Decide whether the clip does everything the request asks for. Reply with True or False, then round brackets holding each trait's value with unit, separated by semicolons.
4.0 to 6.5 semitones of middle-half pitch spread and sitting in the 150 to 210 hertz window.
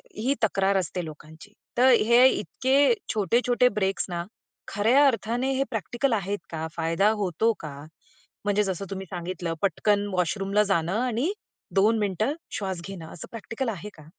True (4.3 semitones; 205 Hz)